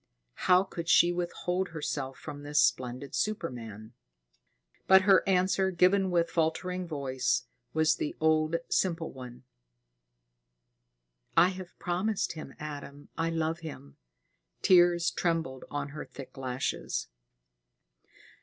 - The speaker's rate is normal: No, slow, 115 wpm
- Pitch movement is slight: No, average, 4.4 semitones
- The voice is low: No, medium, 160 Hz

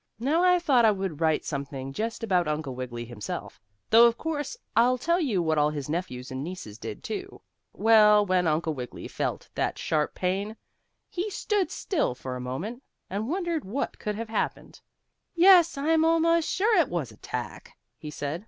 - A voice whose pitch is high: Yes, high, 205 Hz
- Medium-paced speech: Yes, average, 180 wpm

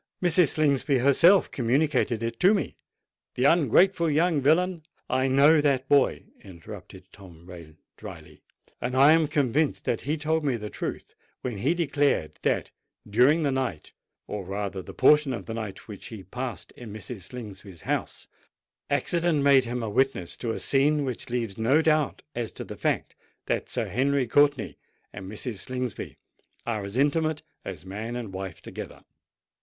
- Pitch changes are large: Yes, wide, 5.7 semitones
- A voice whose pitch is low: Yes, low, 130 Hz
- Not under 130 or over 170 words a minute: Yes, average, 160 wpm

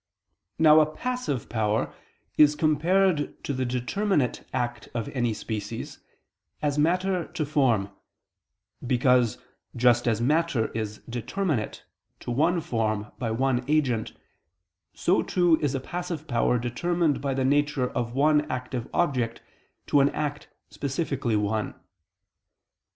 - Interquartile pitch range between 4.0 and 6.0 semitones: Yes, average, 4.5 semitones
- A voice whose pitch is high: No, low, 135 Hz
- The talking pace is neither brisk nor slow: No, slow, 125 wpm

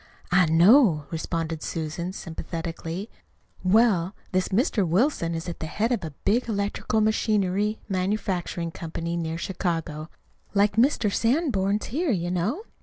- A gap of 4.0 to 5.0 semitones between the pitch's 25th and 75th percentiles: Yes, average, 4.4 semitones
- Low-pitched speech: No, medium, 185 Hz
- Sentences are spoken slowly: Yes, slow, 130 wpm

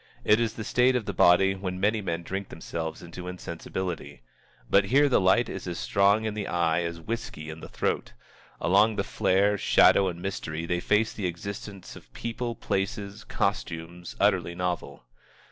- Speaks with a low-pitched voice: Yes, very low, 95 Hz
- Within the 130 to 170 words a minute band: No, average, 180 wpm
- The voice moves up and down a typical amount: Yes, average, 3.4 semitones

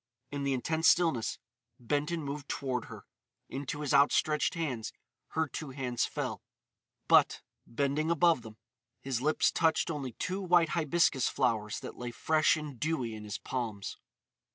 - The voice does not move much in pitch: No, average, 4.3 semitones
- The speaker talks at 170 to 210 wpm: No, average, 150 wpm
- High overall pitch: No, medium, 140 Hz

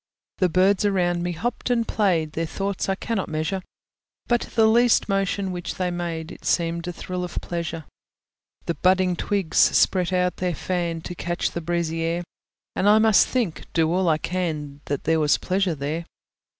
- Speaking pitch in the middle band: Yes, medium, 175 Hz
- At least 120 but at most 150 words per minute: No, average, 180 wpm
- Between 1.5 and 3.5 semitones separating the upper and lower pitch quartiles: Yes, average, 2.7 semitones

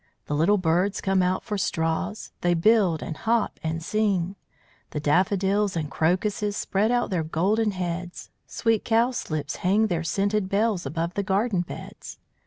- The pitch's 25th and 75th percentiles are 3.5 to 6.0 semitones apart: Yes, average, 3.8 semitones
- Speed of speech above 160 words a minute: No, average, 155 wpm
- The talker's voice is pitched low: No, high, 190 Hz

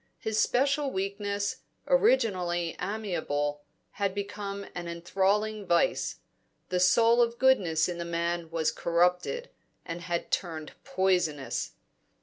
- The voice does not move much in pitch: No, average, 3.8 semitones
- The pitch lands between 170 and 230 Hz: Yes, medium, 185 Hz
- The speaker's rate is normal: No, slow, 115 wpm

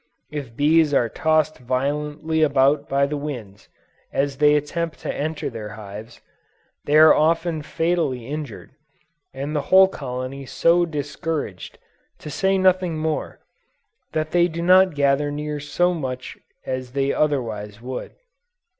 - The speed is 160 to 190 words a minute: No, slow, 135 wpm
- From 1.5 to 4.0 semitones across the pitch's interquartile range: Yes, average, 3.1 semitones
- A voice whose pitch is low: No, medium, 150 Hz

